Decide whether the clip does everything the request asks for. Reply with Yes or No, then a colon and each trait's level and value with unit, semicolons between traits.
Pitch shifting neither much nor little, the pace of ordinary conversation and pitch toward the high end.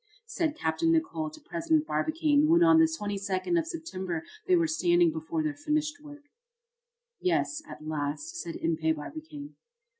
No: wide, 8.6 semitones; average, 150 wpm; very high, 305 Hz